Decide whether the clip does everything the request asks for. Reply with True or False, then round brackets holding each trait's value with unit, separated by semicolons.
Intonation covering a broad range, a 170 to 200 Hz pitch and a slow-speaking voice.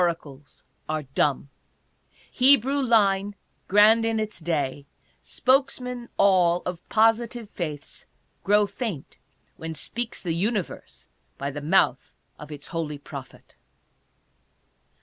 True (7.0 semitones; 190 Hz; 110 wpm)